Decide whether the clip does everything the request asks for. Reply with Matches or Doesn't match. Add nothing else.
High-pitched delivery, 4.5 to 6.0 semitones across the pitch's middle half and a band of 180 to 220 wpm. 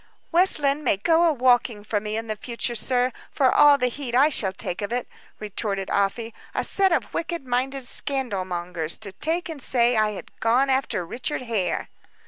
Matches